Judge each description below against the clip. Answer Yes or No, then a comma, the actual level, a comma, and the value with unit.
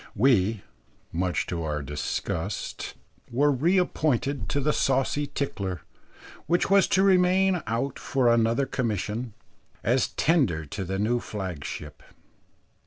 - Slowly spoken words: Yes, slow, 115 wpm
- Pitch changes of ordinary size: No, wide, 7.2 semitones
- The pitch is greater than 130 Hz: No, low, 120 Hz